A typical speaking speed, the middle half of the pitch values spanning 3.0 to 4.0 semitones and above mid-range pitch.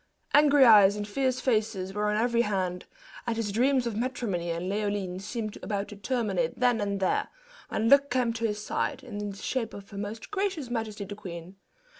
Yes: average, 195 wpm; average, 3.5 semitones; high, 215 Hz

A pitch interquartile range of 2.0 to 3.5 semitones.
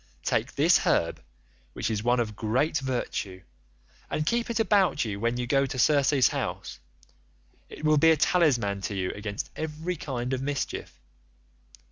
No: wide, 5.5 semitones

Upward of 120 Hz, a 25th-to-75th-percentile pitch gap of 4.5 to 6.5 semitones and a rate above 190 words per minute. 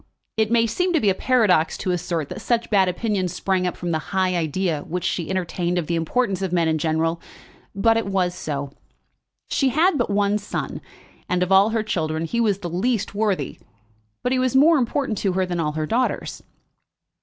Yes: high, 190 Hz; average, 4.8 semitones; average, 200 wpm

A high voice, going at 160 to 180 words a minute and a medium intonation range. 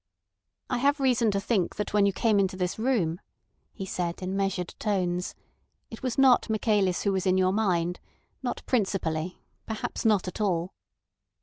Yes: high, 195 Hz; average, 165 wpm; average, 3.4 semitones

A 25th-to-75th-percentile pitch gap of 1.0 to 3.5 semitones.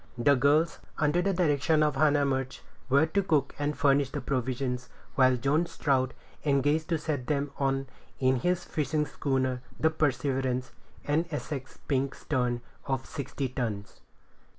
Yes: narrow, 2.6 semitones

